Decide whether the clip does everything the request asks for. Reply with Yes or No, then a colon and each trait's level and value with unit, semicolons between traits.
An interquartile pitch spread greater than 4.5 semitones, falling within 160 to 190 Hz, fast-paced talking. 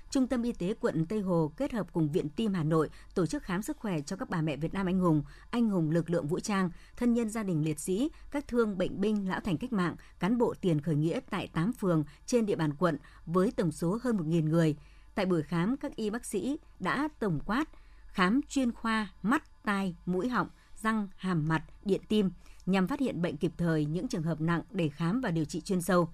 No: average, 5.1 semitones; medium, 185 Hz; average, 240 wpm